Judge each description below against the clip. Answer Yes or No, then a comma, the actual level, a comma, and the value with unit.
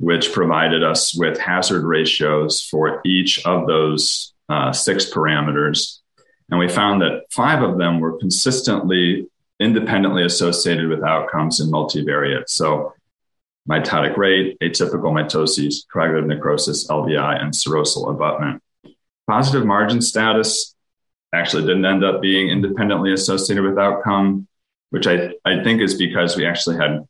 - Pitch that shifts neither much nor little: Yes, average, 4.0 semitones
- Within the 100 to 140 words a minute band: Yes, slow, 135 wpm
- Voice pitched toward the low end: Yes, very low, 90 Hz